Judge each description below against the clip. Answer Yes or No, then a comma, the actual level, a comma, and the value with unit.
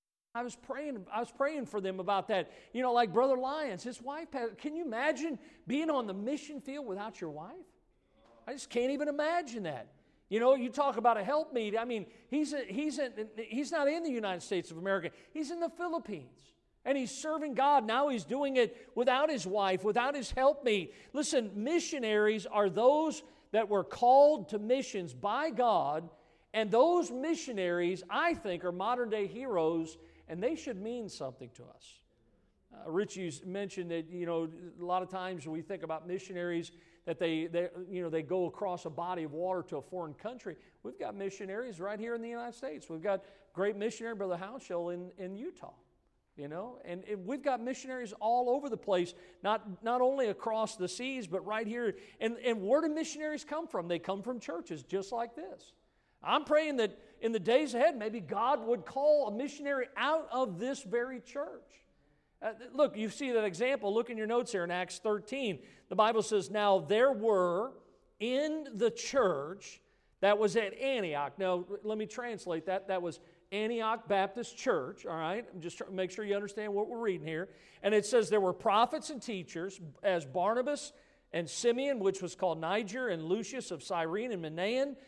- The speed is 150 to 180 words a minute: No, average, 195 wpm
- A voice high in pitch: Yes, high, 220 Hz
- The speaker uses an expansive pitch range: Yes, wide, 6.0 semitones